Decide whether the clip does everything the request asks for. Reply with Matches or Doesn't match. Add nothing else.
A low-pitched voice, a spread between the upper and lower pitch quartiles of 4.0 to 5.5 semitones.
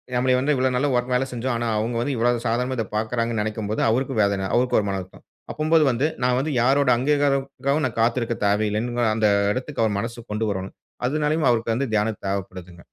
Doesn't match